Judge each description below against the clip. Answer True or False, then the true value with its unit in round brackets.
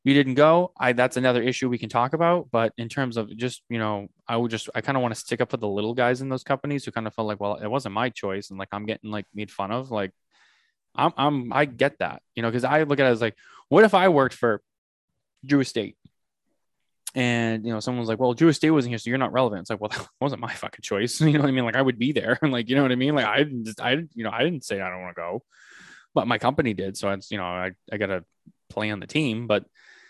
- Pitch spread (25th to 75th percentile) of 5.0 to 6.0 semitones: False (4.2 semitones)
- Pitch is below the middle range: True (120 Hz)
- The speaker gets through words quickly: True (290 wpm)